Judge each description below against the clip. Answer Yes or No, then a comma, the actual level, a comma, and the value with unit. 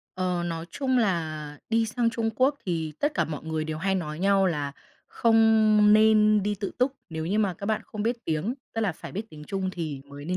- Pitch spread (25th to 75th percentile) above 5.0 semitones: Yes, wide, 5.5 semitones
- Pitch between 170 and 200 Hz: Yes, high, 190 Hz